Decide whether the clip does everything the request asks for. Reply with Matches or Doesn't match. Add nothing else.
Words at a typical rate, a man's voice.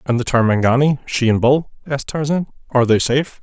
Matches